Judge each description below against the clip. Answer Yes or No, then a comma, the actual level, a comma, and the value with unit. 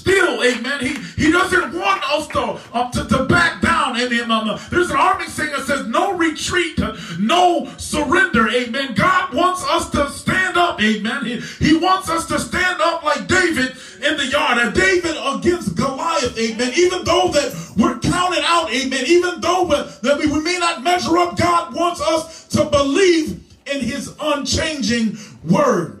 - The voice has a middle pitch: No, very high, 300 Hz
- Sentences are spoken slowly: No, average, 175 wpm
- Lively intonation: Yes, wide, 5.8 semitones